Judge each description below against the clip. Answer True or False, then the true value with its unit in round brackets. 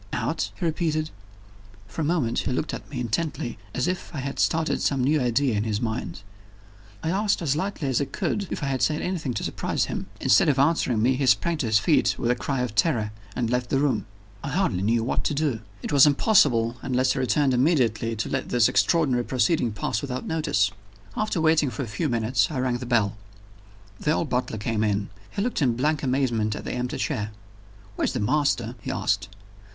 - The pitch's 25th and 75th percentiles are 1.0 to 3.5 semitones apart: False (4.8 semitones)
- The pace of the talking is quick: True (210 wpm)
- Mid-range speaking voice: False (130 Hz)